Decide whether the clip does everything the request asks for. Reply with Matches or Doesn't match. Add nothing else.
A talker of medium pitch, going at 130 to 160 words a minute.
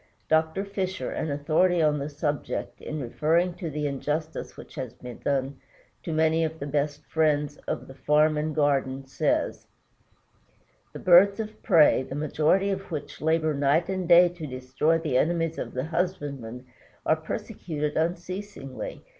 Matches